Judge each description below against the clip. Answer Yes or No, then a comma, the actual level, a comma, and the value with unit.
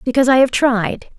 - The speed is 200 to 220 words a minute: Yes, fast, 205 wpm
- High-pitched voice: Yes, very high, 250 Hz